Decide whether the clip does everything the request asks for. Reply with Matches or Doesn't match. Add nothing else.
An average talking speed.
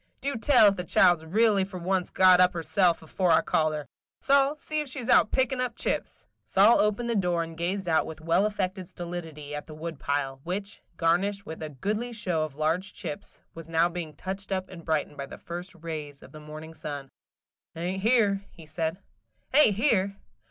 Doesn't match